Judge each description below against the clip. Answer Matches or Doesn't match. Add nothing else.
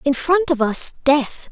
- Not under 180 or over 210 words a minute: Matches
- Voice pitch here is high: Matches